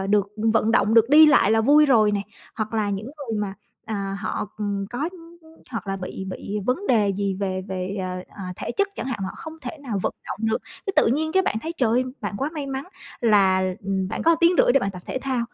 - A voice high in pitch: Yes, high, 220 Hz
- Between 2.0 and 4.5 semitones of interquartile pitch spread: No, average, 5.2 semitones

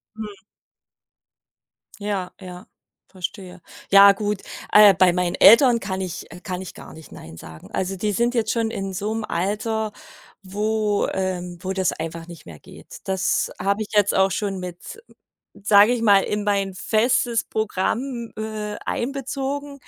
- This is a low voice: No, high, 200 Hz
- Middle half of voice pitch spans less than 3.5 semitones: Yes, average, 2.8 semitones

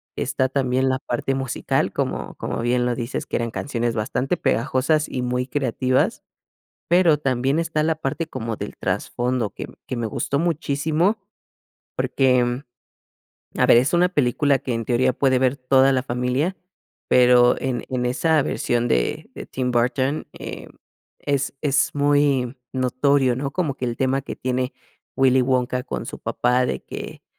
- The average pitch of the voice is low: Yes, low, 130 Hz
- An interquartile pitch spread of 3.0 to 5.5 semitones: No, narrow, 2.4 semitones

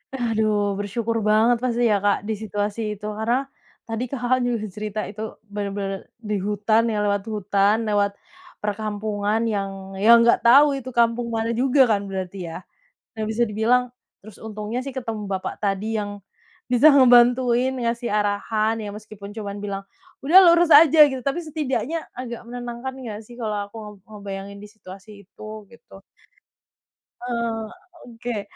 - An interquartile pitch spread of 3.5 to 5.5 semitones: No, average, 2.8 semitones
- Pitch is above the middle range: Yes, high, 220 Hz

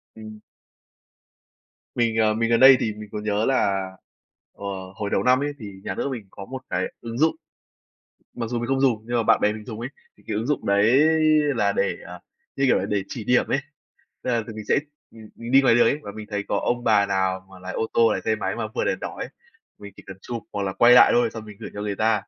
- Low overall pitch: Yes, low, 110 Hz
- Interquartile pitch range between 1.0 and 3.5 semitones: Yes, average, 2.8 semitones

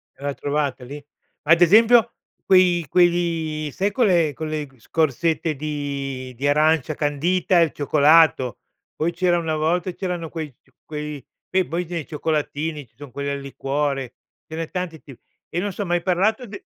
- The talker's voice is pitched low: No, medium, 155 Hz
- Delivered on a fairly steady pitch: No, average, 3.4 semitones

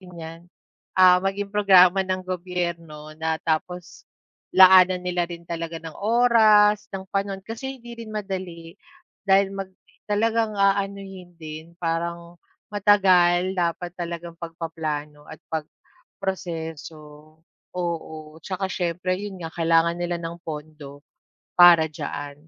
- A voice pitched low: No, medium, 175 Hz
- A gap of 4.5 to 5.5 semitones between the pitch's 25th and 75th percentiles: No, average, 2.9 semitones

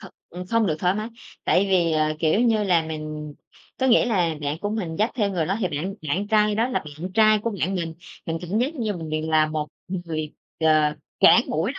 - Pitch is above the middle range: No, medium, 180 Hz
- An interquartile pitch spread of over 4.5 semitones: Yes, average, 5.2 semitones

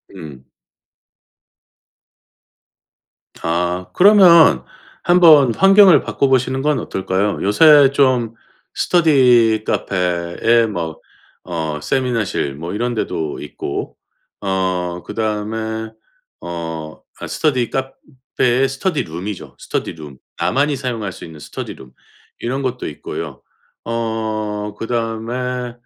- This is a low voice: Yes, low, 115 Hz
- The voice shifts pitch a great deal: Yes, wide, 6.7 semitones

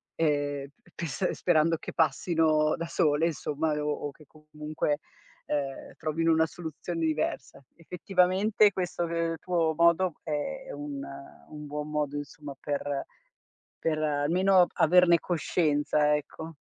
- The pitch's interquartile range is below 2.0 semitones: No, narrow, 2.4 semitones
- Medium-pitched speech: Yes, medium, 155 Hz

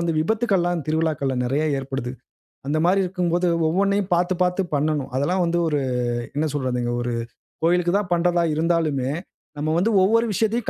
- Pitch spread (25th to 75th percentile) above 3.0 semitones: Yes, average, 3.7 semitones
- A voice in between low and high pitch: Yes, medium, 170 Hz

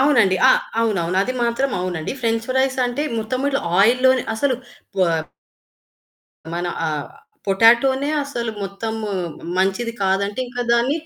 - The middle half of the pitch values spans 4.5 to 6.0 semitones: Yes, average, 5.1 semitones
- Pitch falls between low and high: No, high, 230 Hz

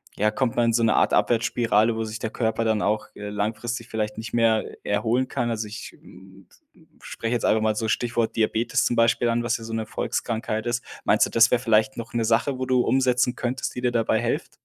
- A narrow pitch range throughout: Yes, narrow, 1.5 semitones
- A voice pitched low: Yes, low, 115 Hz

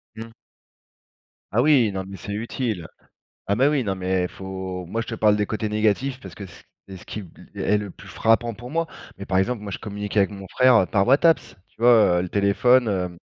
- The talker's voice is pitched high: No, low, 105 Hz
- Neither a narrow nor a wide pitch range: Yes, average, 3.6 semitones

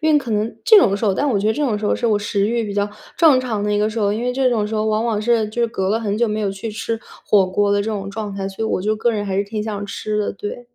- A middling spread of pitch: No, narrow, 2.2 semitones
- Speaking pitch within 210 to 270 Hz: Yes, high, 215 Hz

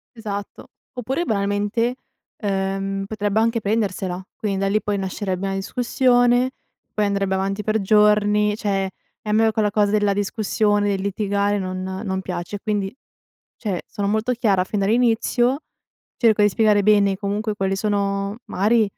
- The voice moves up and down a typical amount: No, narrow, 1.8 semitones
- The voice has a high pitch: Yes, high, 205 Hz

